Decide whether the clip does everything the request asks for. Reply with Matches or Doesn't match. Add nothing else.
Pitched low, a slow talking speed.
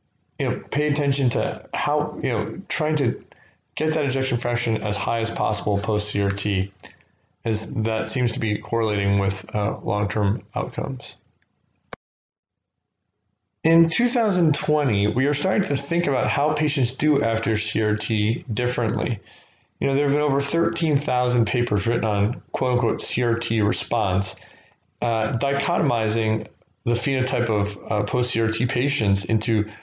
Matches